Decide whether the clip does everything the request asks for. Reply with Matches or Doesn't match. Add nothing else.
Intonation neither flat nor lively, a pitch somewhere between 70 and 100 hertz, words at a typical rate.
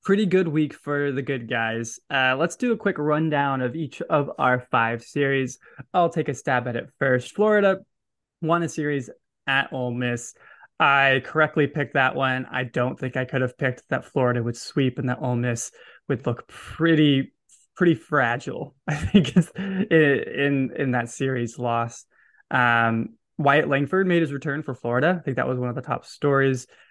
Doesn't match